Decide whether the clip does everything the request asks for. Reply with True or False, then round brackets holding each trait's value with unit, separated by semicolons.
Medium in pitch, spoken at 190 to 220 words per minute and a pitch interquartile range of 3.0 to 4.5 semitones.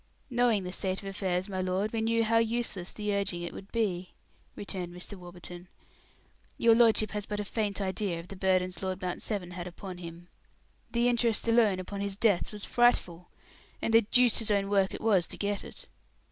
False (200 Hz; 200 wpm; 3.4 semitones)